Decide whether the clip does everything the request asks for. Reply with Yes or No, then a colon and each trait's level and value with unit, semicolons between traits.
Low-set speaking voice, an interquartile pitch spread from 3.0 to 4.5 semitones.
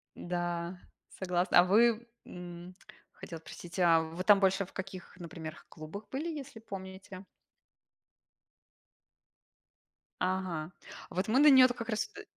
No: medium, 185 Hz; average, 3.6 semitones